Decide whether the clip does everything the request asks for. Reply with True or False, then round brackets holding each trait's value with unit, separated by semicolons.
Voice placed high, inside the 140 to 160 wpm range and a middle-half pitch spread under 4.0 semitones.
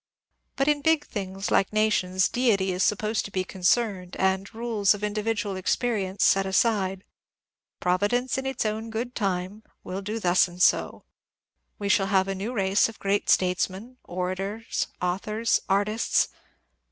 True (200 Hz; 155 wpm; 2.9 semitones)